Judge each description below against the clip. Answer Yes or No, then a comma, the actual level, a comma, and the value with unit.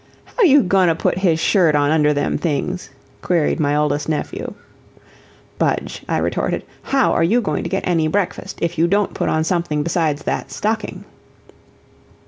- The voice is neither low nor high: Yes, medium, 170 Hz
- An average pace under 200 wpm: Yes, average, 170 wpm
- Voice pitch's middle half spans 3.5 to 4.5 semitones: Yes, average, 4.0 semitones